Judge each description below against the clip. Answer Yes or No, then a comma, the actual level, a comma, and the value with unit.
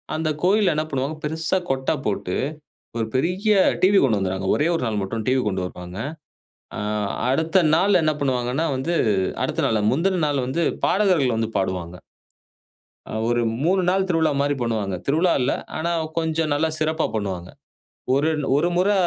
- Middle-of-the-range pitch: Yes, medium, 145 Hz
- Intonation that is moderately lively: No, wide, 6.8 semitones